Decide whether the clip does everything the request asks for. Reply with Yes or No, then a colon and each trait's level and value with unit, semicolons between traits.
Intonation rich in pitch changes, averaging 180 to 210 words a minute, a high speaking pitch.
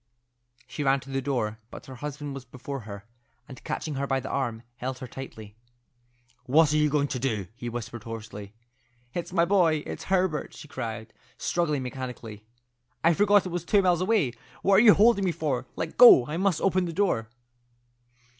No: wide, 6.0 semitones; average, 190 wpm; medium, 140 Hz